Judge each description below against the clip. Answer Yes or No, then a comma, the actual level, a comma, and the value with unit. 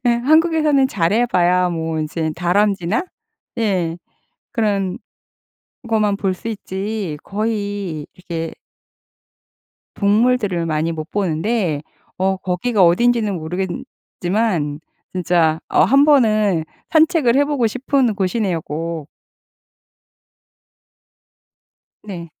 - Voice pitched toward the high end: Yes, high, 195 Hz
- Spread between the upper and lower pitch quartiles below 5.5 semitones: Yes, average, 5.1 semitones